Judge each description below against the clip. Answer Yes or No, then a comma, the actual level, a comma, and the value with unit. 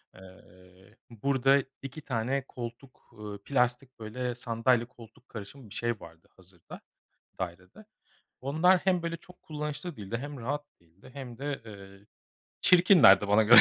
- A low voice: Yes, low, 120 Hz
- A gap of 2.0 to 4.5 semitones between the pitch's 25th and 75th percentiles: No, wide, 5.4 semitones